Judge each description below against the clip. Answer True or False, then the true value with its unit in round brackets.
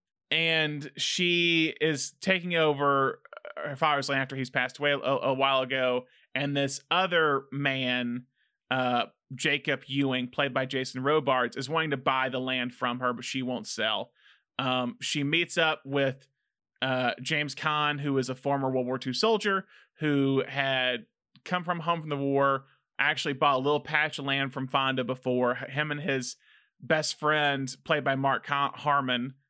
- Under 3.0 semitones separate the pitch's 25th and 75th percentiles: True (2.5 semitones)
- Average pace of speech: True (165 wpm)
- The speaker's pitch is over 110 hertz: True (135 Hz)